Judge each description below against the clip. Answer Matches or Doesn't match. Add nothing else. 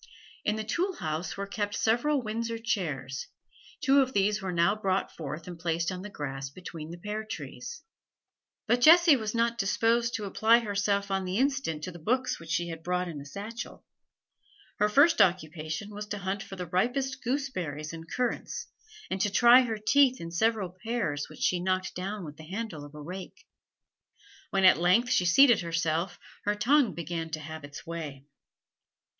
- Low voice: Doesn't match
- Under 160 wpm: Doesn't match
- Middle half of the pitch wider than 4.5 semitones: Matches